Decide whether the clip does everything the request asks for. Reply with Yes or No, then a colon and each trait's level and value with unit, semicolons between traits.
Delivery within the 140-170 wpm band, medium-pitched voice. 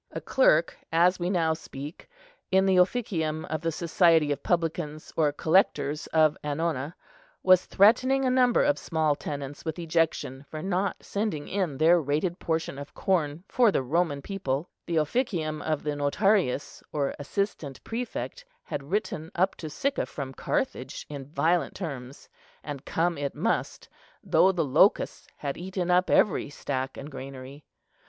Yes: average, 150 wpm; medium, 160 Hz